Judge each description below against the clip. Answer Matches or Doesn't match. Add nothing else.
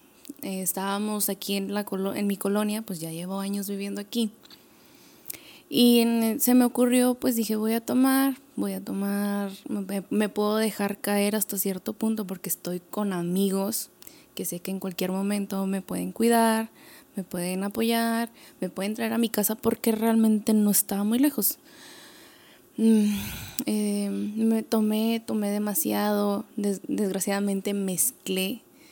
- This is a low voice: Doesn't match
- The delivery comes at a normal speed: Matches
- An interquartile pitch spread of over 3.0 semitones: Doesn't match